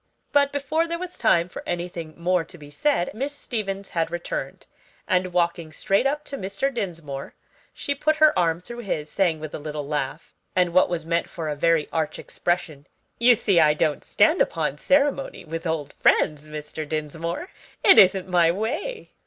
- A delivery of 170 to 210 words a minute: Yes, average, 180 wpm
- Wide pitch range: Yes, wide, 7.1 semitones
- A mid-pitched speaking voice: Yes, medium, 175 Hz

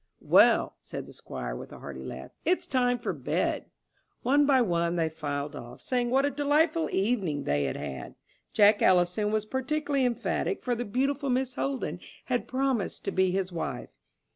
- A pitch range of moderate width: No, wide, 7.7 semitones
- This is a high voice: Yes, high, 235 Hz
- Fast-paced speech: No, average, 175 wpm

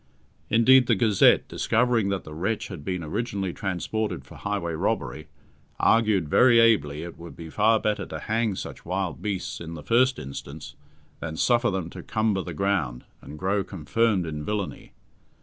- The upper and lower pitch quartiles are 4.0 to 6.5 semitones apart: Yes, average, 5.0 semitones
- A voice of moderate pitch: No, very low, 95 Hz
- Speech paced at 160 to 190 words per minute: Yes, average, 165 wpm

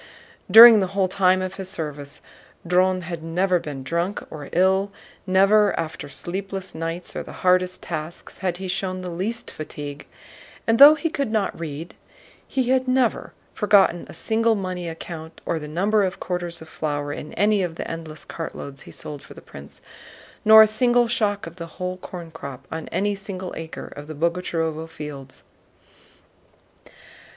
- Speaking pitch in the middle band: Yes, medium, 180 Hz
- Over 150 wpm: Yes, average, 170 wpm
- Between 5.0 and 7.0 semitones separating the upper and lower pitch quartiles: No, average, 3.7 semitones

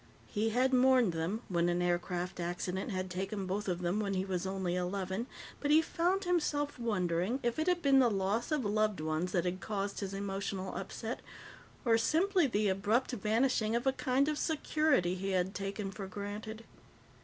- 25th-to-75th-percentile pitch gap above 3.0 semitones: Yes, average, 5.1 semitones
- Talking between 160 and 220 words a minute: Yes, average, 185 wpm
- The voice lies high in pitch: Yes, high, 205 Hz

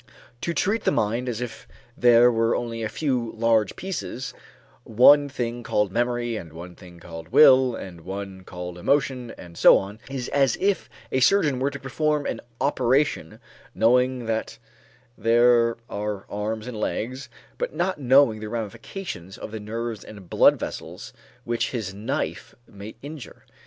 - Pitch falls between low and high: No, low, 115 Hz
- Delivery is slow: No, average, 155 wpm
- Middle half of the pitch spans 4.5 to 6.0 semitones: No, average, 3.9 semitones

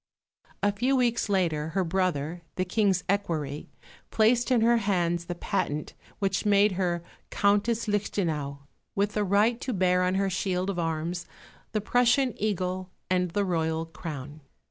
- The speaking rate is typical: Yes, average, 150 wpm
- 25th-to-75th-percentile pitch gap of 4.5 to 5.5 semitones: No, average, 3.4 semitones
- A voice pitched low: No, high, 190 Hz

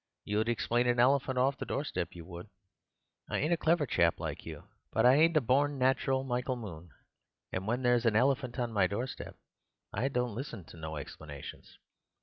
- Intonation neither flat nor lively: Yes, average, 4.6 semitones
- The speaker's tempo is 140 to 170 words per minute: No, average, 185 wpm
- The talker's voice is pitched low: Yes, low, 125 Hz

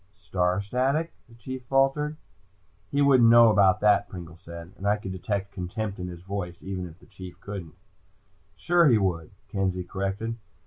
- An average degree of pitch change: Yes, average, 4.3 semitones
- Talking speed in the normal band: Yes, average, 170 wpm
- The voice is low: Yes, low, 100 Hz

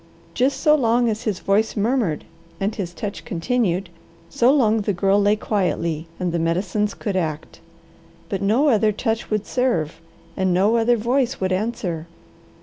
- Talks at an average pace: Yes, average, 160 wpm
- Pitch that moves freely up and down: No, average, 4.3 semitones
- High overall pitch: Yes, high, 205 Hz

